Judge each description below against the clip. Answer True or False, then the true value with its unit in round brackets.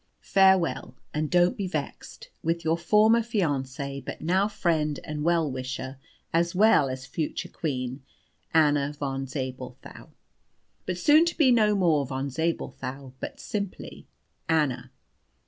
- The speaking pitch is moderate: True (155 Hz)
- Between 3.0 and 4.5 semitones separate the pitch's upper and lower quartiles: False (5.2 semitones)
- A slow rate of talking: True (130 wpm)